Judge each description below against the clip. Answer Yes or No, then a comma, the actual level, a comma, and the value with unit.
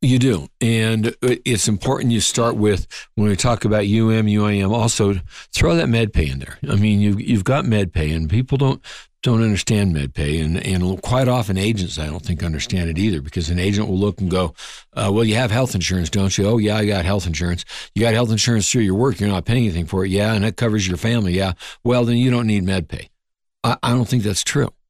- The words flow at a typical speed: No, fast, 240 wpm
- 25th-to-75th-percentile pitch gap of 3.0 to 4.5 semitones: Yes, average, 3.9 semitones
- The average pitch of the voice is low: Yes, low, 105 Hz